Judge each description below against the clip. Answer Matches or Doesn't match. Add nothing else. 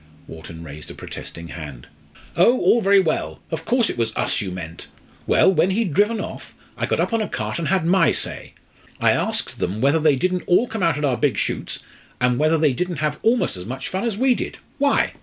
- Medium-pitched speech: Matches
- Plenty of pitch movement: Matches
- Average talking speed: Doesn't match